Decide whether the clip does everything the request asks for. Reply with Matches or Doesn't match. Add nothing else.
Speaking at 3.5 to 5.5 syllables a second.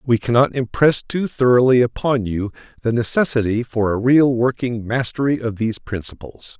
Matches